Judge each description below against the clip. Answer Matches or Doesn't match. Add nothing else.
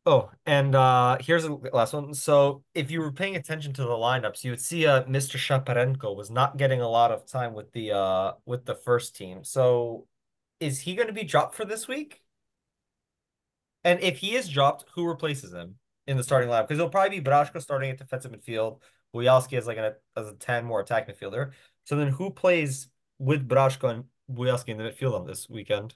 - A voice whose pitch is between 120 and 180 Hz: Matches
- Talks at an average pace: Doesn't match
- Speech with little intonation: Doesn't match